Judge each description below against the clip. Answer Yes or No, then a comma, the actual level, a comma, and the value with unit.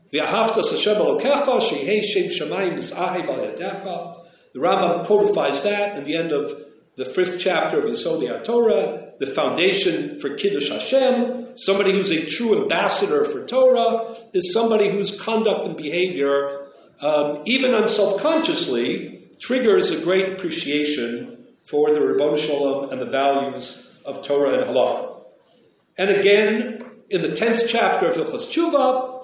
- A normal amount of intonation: No, wide, 7.1 semitones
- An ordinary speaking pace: No, slow, 125 wpm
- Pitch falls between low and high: No, high, 205 Hz